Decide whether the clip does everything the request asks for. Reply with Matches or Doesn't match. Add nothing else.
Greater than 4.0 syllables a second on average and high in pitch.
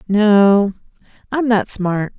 Doesn't match